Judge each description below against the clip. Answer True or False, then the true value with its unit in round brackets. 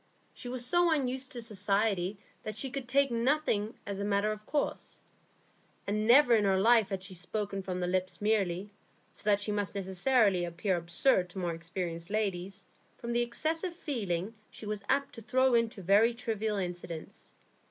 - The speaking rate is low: False (175 wpm)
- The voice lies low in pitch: False (210 Hz)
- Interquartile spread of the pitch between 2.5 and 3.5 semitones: False (4.2 semitones)